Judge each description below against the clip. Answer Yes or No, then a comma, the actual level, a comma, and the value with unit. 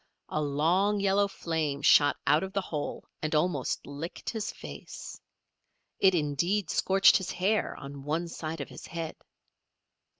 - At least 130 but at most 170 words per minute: Yes, average, 145 wpm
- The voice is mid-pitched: Yes, medium, 165 Hz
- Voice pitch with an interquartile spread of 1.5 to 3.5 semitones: No, average, 4.4 semitones